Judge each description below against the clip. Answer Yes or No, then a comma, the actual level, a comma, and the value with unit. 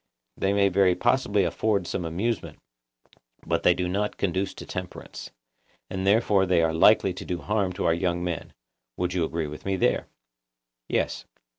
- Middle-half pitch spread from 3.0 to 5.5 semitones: No, narrow, 2.5 semitones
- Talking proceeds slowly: No, average, 165 wpm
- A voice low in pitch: Yes, very low, 95 Hz